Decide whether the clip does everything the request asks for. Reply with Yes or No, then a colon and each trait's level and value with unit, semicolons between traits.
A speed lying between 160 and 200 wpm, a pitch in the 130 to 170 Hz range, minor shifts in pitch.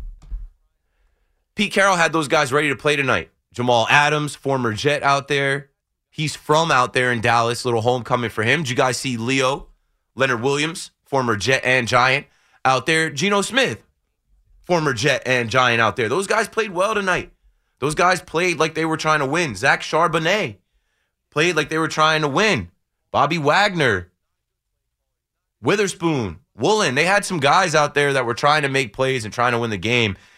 No: average, 180 wpm; medium, 140 Hz; average, 4.6 semitones